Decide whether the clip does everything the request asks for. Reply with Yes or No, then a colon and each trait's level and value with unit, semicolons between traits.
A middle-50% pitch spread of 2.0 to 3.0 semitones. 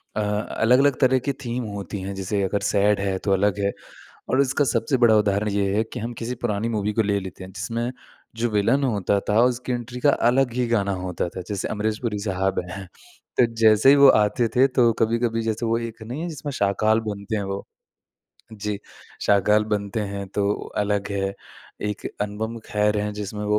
Yes: narrow, 2.6 semitones